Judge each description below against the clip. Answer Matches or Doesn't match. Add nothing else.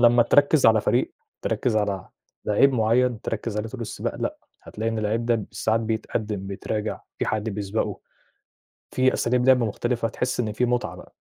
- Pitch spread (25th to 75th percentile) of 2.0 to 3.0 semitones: Matches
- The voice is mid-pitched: Doesn't match